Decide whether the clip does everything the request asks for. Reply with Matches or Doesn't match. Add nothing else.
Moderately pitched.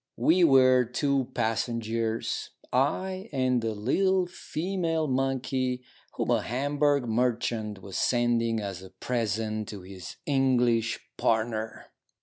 Doesn't match